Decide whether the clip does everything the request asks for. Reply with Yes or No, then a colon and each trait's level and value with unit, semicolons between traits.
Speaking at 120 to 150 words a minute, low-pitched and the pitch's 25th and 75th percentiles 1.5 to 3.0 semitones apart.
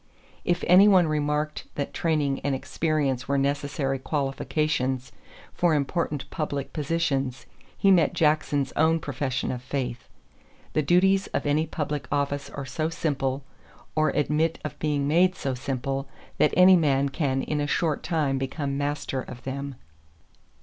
No: average, 145 wpm; medium, 145 Hz; narrow, 2.5 semitones